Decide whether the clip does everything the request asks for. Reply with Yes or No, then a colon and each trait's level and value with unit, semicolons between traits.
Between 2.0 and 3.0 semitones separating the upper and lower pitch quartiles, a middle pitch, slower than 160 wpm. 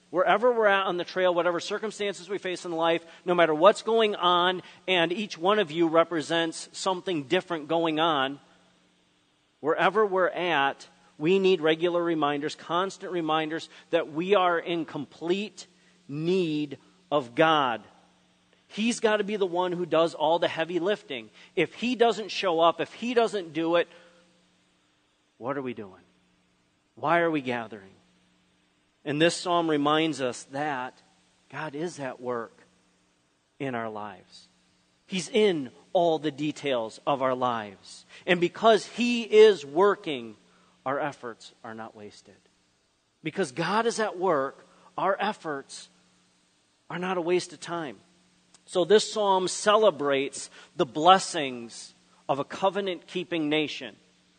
No: wide, 5.6 semitones; medium, 165 Hz; average, 140 wpm